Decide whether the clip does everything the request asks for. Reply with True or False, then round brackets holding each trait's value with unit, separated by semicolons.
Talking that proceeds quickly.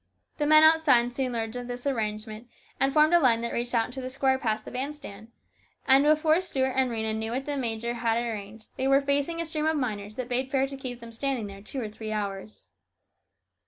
True (235 wpm)